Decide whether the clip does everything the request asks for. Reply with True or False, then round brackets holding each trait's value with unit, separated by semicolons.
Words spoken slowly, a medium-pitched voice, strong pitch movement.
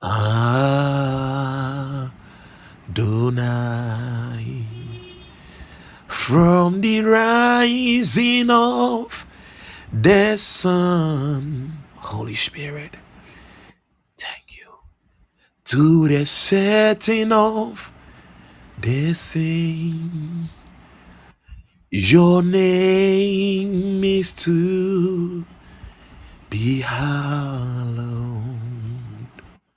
True (50 wpm; 145 Hz; 7.9 semitones)